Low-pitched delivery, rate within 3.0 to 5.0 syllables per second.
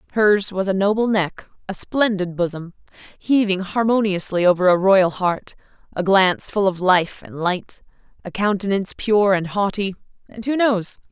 No: high, 195 Hz; 4.7 syllables/s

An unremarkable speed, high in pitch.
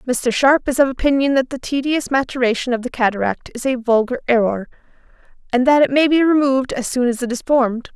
No: fast, 210 wpm; very high, 255 Hz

